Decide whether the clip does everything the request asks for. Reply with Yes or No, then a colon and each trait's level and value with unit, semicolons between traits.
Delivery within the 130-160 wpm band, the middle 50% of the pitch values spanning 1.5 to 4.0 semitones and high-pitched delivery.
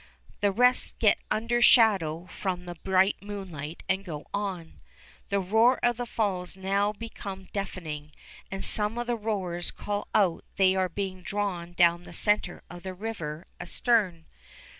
Yes: average, 155 wpm; average, 3.1 semitones; high, 195 Hz